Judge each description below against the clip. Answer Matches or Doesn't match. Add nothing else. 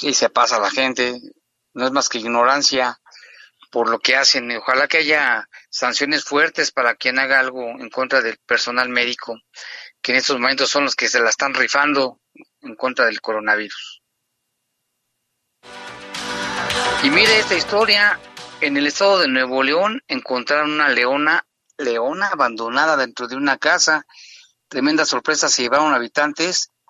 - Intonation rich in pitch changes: Doesn't match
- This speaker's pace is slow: Doesn't match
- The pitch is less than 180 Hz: Matches